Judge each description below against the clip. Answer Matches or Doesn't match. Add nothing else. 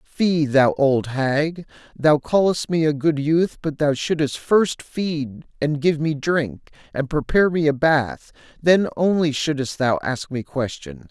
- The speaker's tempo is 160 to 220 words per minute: Matches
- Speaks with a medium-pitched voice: Matches